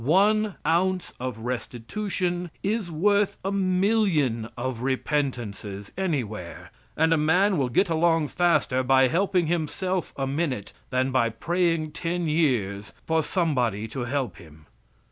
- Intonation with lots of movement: Yes, wide, 6.2 semitones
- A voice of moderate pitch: Yes, medium, 155 Hz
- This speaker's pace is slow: Yes, slow, 130 wpm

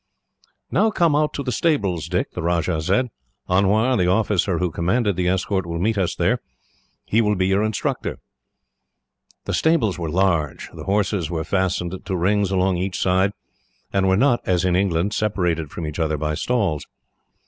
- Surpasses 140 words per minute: Yes, average, 175 wpm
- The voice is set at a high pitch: No, very low, 95 Hz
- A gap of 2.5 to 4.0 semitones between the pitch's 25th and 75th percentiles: Yes, average, 3.3 semitones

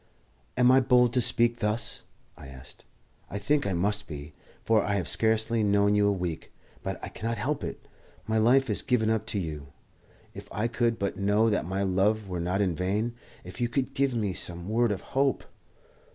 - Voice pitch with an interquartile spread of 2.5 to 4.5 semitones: Yes, average, 3.5 semitones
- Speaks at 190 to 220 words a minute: Yes, average, 200 wpm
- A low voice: Yes, low, 105 Hz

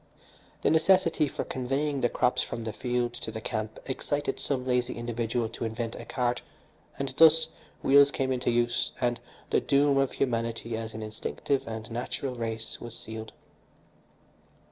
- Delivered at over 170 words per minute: No, average, 160 wpm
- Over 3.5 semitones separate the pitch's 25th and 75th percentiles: No, average, 3.2 semitones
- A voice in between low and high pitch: No, low, 120 Hz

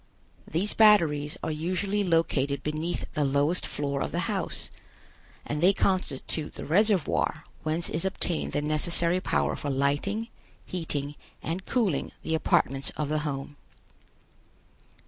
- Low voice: No, medium, 155 Hz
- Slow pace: Yes, slow, 130 wpm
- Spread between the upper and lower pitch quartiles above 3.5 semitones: Yes, average, 4.0 semitones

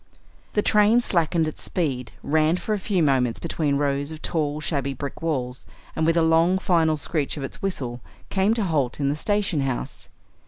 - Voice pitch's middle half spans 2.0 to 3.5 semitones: No, average, 4.3 semitones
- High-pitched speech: No, medium, 155 Hz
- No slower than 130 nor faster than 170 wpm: No, average, 190 wpm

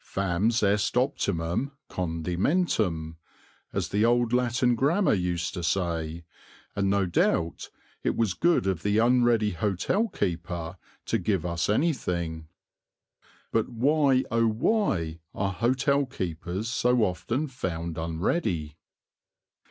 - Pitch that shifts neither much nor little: No, wide, 6.3 semitones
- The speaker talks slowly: Yes, slow, 115 wpm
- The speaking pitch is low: Yes, low, 100 Hz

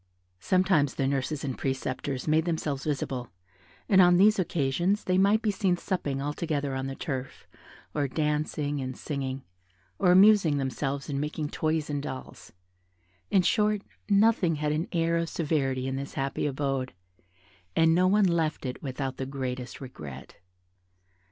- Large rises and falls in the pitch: No, average, 4.5 semitones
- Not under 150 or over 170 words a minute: Yes, average, 155 wpm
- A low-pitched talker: No, medium, 150 Hz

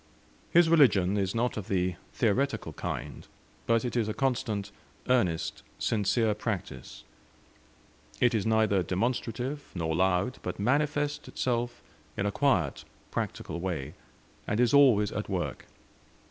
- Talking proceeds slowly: Yes, slow, 130 wpm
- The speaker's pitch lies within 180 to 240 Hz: No, low, 110 Hz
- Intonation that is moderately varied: Yes, average, 4.7 semitones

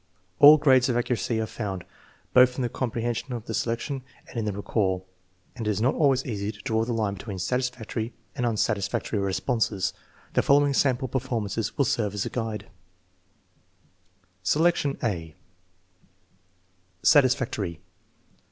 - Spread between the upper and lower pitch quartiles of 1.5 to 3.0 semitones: No, average, 3.8 semitones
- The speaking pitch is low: Yes, low, 115 Hz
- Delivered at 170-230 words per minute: No, average, 150 wpm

